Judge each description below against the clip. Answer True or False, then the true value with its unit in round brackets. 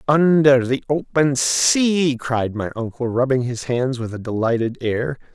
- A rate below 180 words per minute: True (155 wpm)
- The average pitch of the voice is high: False (130 Hz)